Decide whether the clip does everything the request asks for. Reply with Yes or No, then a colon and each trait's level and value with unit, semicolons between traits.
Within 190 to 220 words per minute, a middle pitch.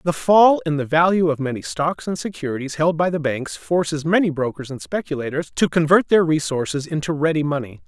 Yes: average, 200 wpm; medium, 150 Hz